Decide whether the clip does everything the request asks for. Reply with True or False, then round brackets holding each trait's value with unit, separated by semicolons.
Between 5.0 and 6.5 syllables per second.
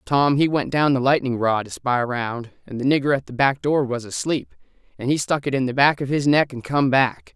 True (5.4 syllables/s)